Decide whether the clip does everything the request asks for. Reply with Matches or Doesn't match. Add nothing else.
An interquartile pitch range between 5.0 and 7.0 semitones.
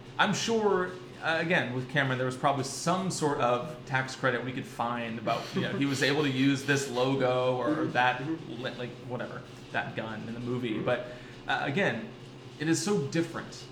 Doesn't match